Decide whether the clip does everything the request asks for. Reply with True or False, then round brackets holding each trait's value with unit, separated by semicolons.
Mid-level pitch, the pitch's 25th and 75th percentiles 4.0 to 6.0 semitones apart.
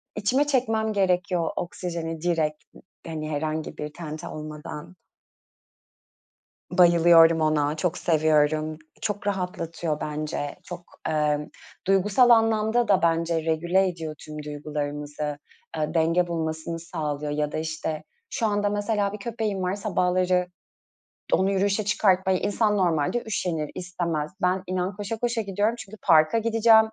True (175 Hz; 4.6 semitones)